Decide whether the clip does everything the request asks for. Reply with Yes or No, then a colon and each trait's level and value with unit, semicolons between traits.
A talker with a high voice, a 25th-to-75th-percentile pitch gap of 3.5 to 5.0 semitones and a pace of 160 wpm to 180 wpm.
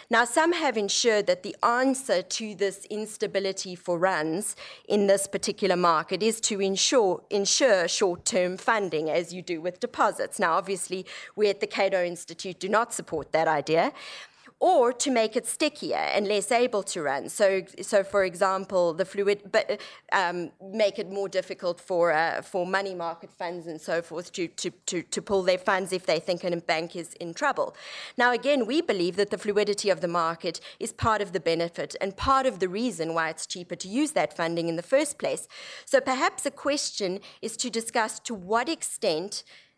No: high, 195 Hz; average, 4.1 semitones; average, 190 wpm